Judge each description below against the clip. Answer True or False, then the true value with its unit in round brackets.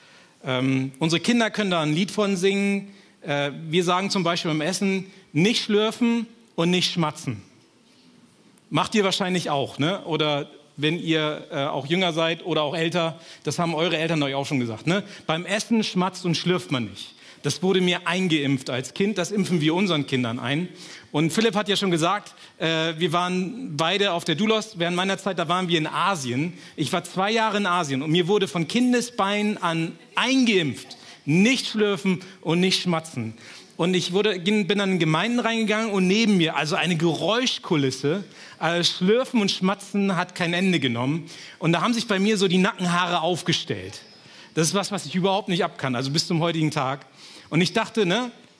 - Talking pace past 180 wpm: True (190 wpm)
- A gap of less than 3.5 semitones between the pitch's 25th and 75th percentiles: False (4.1 semitones)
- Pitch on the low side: False (175 Hz)